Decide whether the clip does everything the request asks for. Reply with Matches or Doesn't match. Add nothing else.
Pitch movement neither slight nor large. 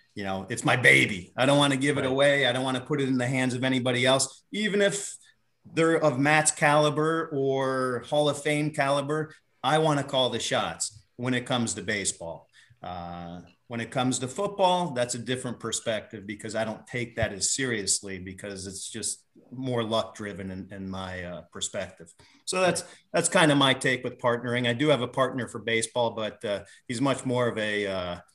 Matches